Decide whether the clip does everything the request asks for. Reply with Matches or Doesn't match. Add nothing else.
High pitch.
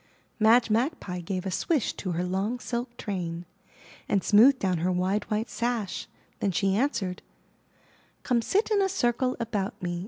Matches